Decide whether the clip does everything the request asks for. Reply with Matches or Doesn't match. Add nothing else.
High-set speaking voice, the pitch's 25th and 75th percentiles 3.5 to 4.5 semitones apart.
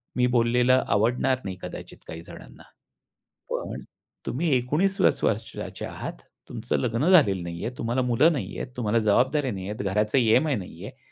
Doesn't match